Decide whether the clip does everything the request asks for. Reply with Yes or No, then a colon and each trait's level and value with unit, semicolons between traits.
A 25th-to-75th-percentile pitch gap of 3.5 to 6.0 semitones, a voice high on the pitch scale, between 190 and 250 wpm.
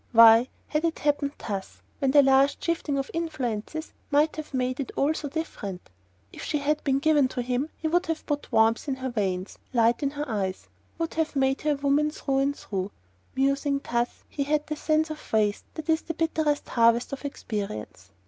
Yes: average, 4.3 semitones; very high, 275 Hz; fast, 205 wpm